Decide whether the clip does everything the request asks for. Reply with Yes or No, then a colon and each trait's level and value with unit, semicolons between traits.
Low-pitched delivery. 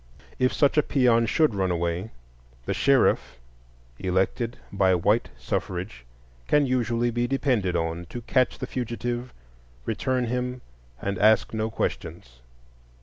Yes: low, 115 Hz